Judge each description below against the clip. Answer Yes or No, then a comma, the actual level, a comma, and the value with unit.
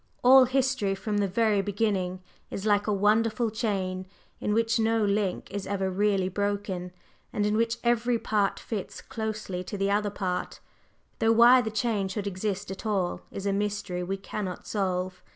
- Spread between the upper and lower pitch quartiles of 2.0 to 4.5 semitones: Yes, narrow, 2.5 semitones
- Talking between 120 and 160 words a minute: No, average, 170 wpm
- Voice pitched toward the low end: No, high, 205 Hz